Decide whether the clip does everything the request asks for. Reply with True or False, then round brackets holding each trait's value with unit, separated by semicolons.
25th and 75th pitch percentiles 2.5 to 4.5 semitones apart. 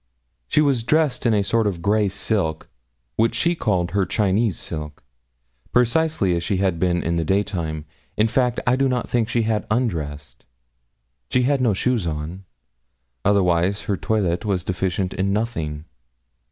False (5.0 semitones)